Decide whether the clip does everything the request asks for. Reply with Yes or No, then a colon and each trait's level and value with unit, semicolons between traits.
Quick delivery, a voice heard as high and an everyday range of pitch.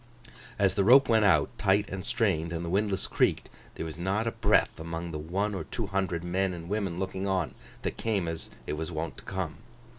No: fast, 215 wpm; very low, 95 Hz; average, 3.3 semitones